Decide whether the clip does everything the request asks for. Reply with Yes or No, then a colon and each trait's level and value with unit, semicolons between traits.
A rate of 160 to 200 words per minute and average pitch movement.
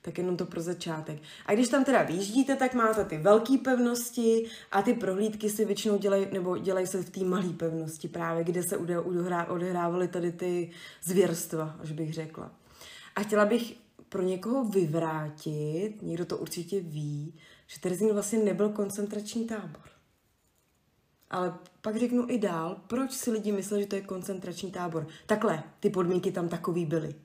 Yes: average, 165 wpm; average, 3.6 semitones